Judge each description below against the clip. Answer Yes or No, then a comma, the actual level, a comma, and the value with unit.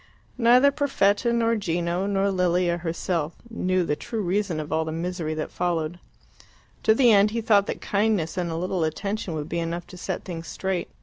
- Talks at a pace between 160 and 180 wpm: No, average, 190 wpm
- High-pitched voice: No, medium, 180 Hz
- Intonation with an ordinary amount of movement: Yes, average, 3.7 semitones